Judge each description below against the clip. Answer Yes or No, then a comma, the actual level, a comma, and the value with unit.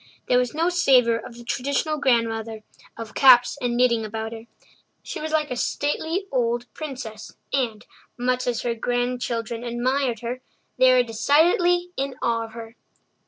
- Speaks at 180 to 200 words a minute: No, average, 160 wpm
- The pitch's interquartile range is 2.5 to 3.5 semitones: Yes, average, 2.9 semitones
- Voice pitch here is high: Yes, high, 245 Hz